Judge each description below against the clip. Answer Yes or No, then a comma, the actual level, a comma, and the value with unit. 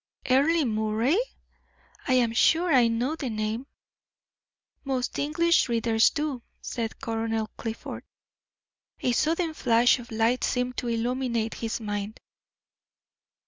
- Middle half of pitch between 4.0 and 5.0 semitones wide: No, average, 3.2 semitones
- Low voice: No, high, 240 Hz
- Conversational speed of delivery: No, slow, 115 wpm